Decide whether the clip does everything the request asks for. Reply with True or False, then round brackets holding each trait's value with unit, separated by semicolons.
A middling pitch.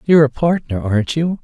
True (145 Hz)